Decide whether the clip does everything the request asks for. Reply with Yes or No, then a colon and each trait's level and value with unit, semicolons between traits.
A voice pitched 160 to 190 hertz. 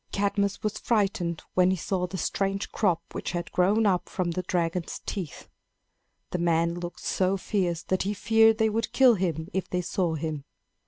Yes: medium, 185 Hz